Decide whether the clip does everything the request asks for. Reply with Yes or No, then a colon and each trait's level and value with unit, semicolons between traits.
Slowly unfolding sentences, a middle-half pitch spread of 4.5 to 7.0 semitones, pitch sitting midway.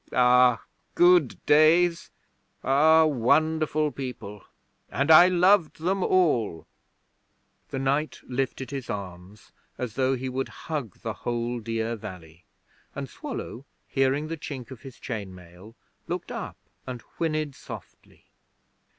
No: slow, 125 wpm; average, 5.3 semitones; low, 130 Hz